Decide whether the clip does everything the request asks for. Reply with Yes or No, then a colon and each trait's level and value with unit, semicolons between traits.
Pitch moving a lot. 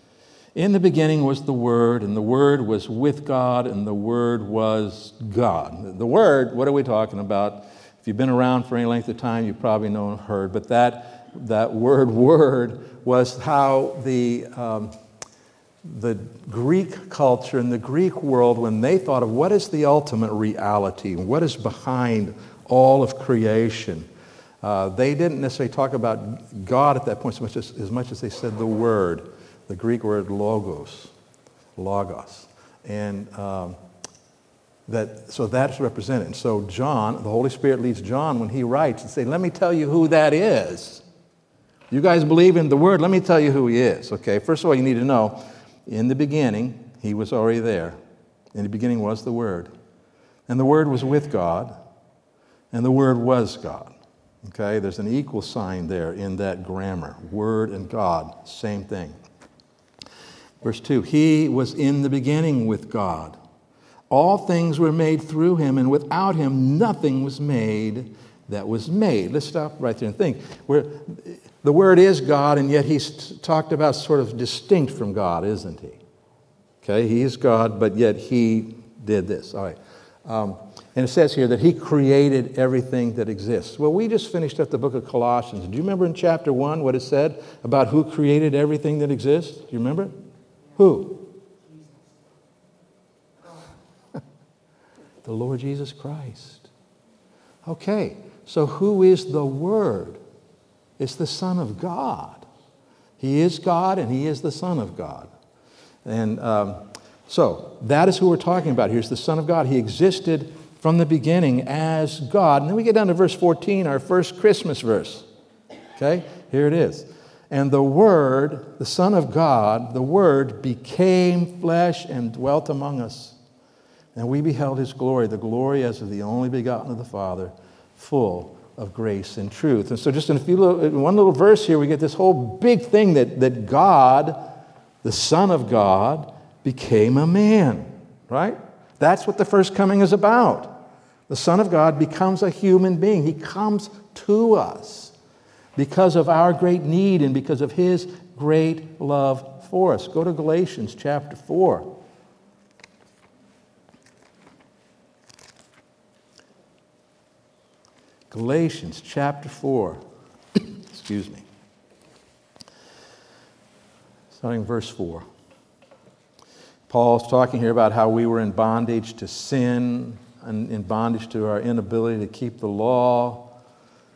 Yes: wide, 5.7 semitones